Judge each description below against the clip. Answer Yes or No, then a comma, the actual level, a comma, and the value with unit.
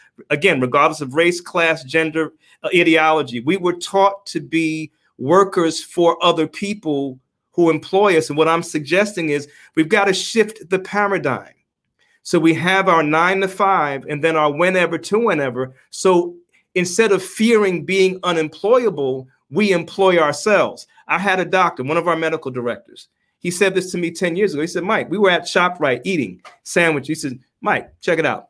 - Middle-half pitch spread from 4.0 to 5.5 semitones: No, average, 3.5 semitones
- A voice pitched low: No, medium, 175 Hz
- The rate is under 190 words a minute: Yes, average, 180 wpm